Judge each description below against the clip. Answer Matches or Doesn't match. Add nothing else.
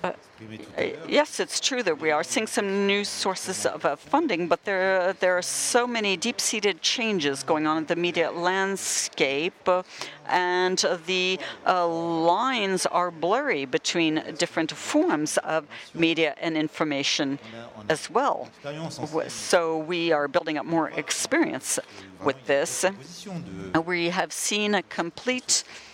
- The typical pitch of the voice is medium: Matches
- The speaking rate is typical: Doesn't match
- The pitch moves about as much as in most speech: Matches